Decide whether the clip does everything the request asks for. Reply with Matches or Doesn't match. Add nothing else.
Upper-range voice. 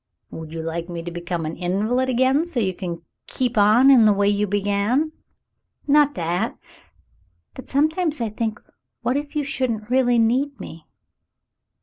Matches